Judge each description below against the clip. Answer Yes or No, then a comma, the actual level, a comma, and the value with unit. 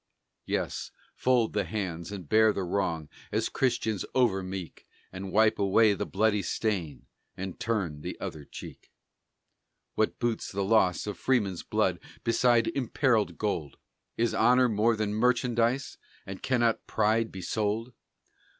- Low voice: Yes, low, 110 Hz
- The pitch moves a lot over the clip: No, average, 3.3 semitones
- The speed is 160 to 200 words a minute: No, average, 140 wpm